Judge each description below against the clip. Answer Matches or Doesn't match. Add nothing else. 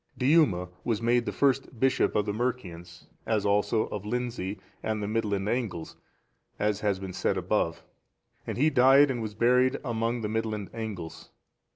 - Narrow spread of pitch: Doesn't match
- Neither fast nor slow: Matches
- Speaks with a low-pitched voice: Matches